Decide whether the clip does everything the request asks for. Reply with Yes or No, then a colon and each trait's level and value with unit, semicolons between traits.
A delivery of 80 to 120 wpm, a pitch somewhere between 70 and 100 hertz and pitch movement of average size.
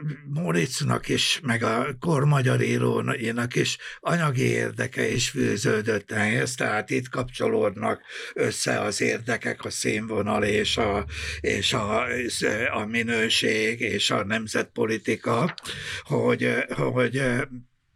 No: average, 110 wpm; low, 120 Hz; average, 3.1 semitones